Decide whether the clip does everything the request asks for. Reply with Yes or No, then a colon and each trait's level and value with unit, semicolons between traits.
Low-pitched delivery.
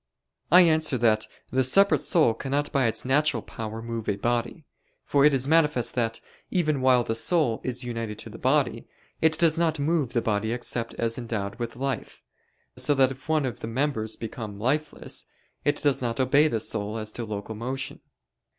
Yes: low, 125 Hz